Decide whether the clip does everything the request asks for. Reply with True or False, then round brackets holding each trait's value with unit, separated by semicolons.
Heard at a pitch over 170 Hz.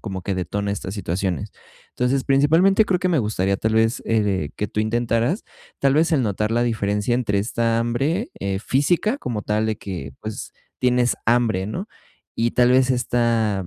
False (115 Hz)